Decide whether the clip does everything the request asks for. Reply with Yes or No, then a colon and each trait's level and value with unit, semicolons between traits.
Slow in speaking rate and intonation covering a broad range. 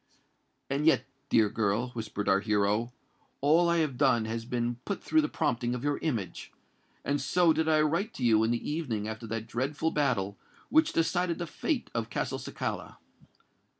No: average, 175 wpm; wide, 6.2 semitones